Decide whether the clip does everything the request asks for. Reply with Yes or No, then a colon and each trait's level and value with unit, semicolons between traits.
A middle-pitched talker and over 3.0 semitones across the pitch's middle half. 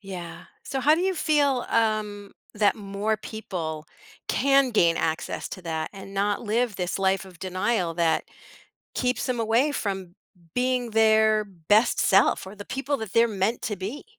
No: high, 210 Hz; average, 4.0 semitones